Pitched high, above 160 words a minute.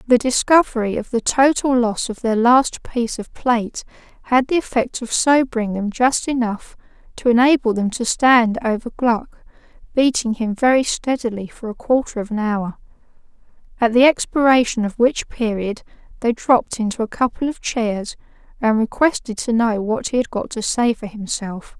Yes: high, 235 Hz; average, 170 wpm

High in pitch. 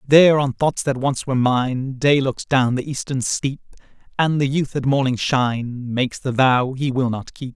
No: low, 135 Hz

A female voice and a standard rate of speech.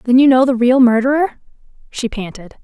Yes: female; average, 180 wpm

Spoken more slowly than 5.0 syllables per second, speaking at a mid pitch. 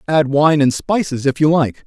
Yes: 4.7 syllables/s; medium, 145 Hz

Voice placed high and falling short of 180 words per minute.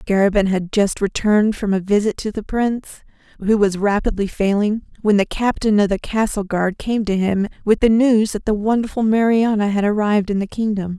No: high, 210 Hz; average, 195 wpm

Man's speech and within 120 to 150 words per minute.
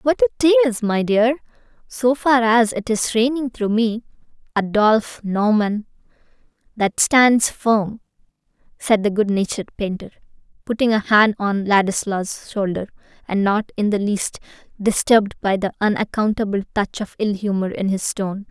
No: female; average, 140 wpm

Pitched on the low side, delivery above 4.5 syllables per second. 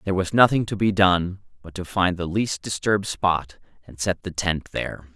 Yes: very low, 95 Hz; 5.1 syllables/s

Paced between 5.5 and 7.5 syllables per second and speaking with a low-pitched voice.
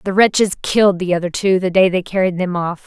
No: 5.9 syllables/s; medium, 185 Hz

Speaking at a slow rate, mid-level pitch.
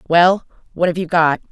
No: average, 200 wpm; medium, 170 Hz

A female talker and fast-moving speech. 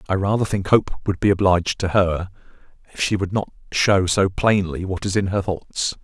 No: male; fast, 210 wpm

